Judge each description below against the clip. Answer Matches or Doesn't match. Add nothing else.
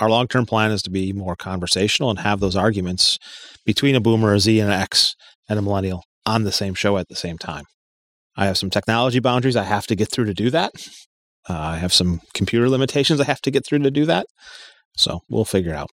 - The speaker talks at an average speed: Doesn't match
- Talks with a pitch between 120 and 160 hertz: Doesn't match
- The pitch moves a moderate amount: Matches